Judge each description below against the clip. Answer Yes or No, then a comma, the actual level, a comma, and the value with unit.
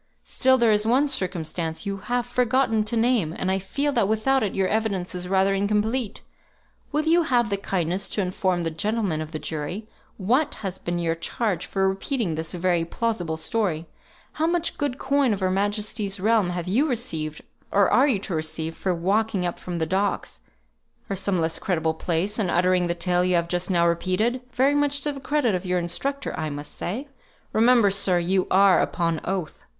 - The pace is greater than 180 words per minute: Yes, average, 195 wpm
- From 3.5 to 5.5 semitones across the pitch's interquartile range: Yes, average, 4.9 semitones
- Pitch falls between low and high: No, high, 195 Hz